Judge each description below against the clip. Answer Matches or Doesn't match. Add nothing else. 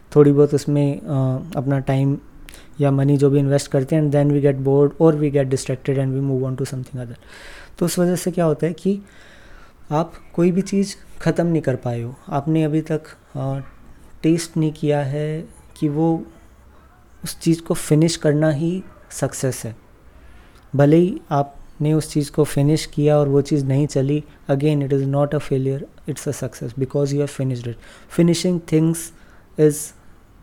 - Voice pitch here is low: Doesn't match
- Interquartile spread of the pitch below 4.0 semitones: Matches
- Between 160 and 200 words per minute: Matches